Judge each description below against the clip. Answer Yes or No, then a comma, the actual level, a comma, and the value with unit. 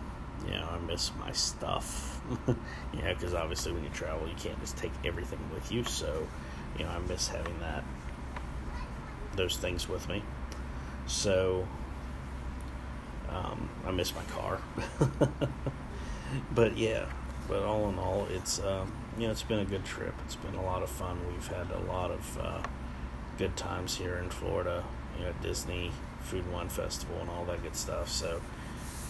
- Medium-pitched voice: No, very low, 80 Hz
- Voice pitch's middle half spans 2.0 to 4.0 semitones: No, average, 5.3 semitones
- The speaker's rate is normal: Yes, average, 170 wpm